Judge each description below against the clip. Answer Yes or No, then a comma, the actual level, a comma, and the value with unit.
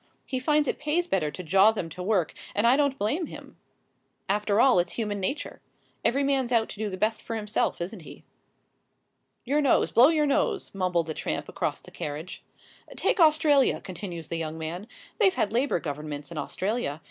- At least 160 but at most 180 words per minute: No, average, 190 wpm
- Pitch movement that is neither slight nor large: No, wide, 7.8 semitones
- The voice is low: No, high, 210 Hz